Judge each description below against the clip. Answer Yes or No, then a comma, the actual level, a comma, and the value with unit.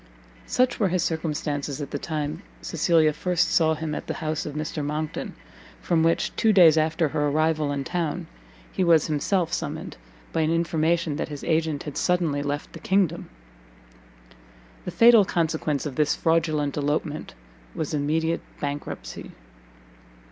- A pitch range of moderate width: No, narrow, 2.2 semitones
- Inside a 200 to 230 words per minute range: No, average, 150 wpm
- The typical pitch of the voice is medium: Yes, medium, 155 Hz